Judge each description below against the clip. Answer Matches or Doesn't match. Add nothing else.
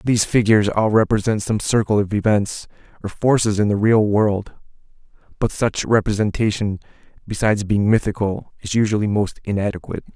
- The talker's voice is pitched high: Doesn't match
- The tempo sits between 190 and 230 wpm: Doesn't match